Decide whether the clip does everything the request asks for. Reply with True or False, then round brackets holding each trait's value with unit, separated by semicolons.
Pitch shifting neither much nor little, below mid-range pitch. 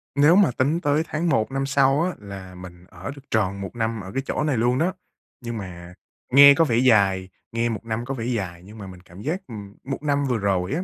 False (6.2 semitones; 115 Hz)